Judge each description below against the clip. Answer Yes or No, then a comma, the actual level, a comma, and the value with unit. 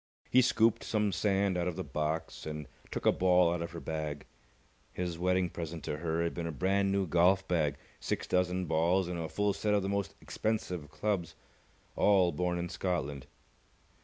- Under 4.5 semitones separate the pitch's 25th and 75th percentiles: Yes, average, 2.8 semitones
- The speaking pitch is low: Yes, very low, 90 Hz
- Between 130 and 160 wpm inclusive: No, average, 190 wpm